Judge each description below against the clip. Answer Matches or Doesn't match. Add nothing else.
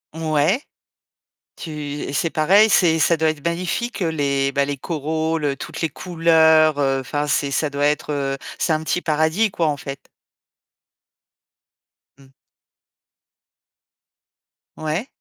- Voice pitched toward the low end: Doesn't match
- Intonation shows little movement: Matches